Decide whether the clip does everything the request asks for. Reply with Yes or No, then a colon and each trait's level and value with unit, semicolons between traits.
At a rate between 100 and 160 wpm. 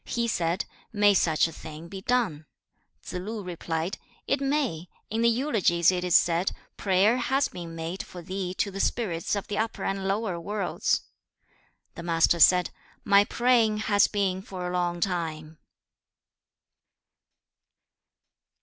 Yes: average, 145 wpm